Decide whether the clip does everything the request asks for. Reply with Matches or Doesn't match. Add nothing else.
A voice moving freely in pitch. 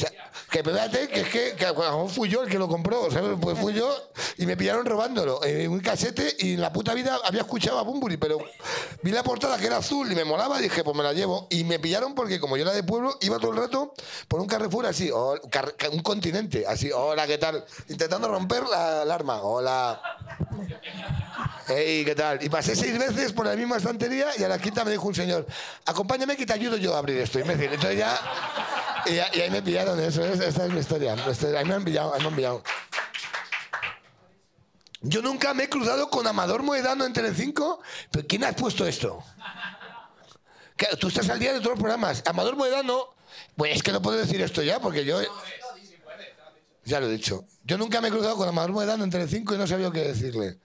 Matches